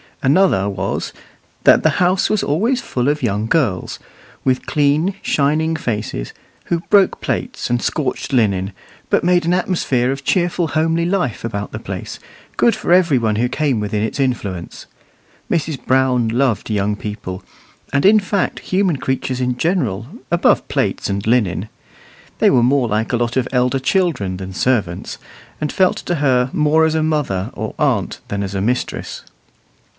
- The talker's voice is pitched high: No, low, 130 Hz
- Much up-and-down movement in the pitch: Yes, wide, 7.0 semitones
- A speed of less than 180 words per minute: Yes, average, 165 wpm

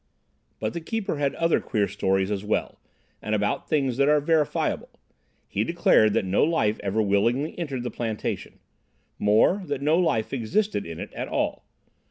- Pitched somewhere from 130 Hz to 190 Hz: No, low, 120 Hz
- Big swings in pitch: Yes, wide, 6.8 semitones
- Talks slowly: No, average, 170 wpm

